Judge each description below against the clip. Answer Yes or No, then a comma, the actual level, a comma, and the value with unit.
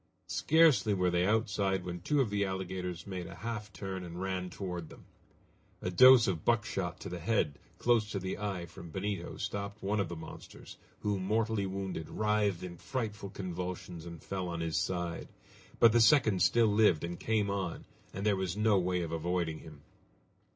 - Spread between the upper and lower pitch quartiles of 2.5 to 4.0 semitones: Yes, average, 3.2 semitones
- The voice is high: No, very low, 95 Hz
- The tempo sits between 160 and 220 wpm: Yes, average, 185 wpm